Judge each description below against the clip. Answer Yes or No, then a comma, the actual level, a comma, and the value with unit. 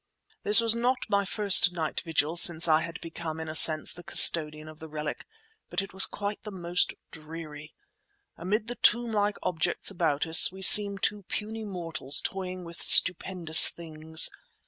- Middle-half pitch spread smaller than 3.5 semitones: No, average, 4.0 semitones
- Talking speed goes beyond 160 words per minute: Yes, average, 170 wpm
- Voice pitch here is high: No, medium, 175 Hz